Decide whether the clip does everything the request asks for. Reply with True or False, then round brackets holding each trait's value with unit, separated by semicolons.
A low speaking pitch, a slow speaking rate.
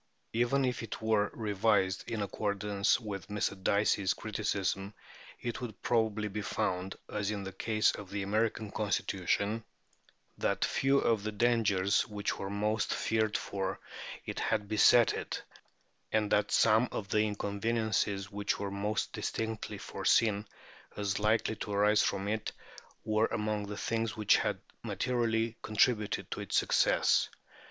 False (105 Hz; 145 wpm)